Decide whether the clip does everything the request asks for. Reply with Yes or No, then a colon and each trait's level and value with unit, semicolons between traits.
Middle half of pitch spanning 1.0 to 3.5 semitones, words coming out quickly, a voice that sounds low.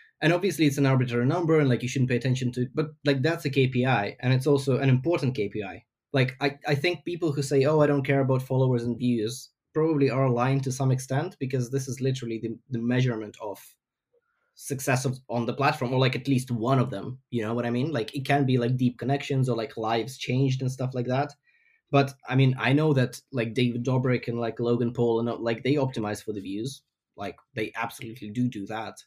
Yes: average, 2.7 semitones; fast, 230 wpm; low, 130 Hz